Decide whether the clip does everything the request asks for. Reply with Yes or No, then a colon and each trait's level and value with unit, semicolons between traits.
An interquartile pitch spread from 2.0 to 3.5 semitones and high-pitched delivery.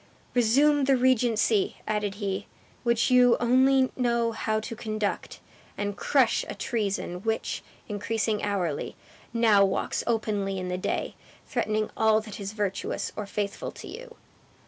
Yes: average, 2.9 semitones; high, 220 Hz